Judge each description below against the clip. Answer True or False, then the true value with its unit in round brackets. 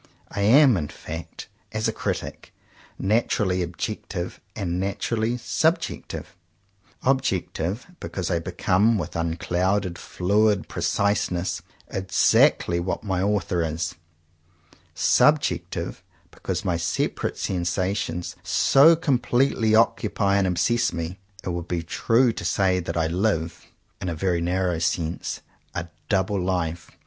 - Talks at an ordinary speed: False (120 wpm)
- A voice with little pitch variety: False (3.8 semitones)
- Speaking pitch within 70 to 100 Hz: True (95 Hz)